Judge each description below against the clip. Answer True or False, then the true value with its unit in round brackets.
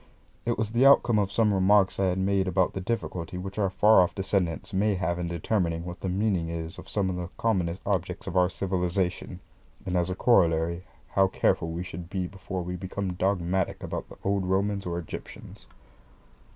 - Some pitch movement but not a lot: False (1.9 semitones)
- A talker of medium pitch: False (95 Hz)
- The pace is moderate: True (195 wpm)